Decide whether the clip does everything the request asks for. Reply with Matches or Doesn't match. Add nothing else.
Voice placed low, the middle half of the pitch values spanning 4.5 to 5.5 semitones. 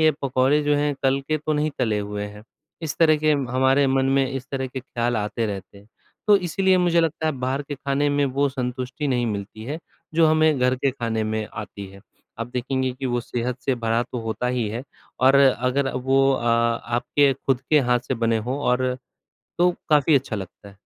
Doesn't match